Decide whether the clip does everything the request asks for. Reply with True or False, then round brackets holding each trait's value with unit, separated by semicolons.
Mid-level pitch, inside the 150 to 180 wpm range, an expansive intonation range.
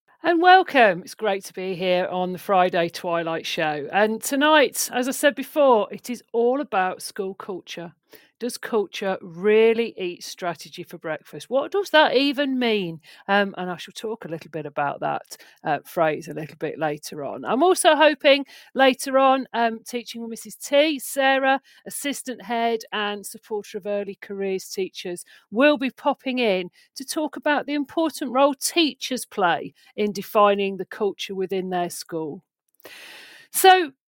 False (225 Hz; 160 wpm; 6.6 semitones)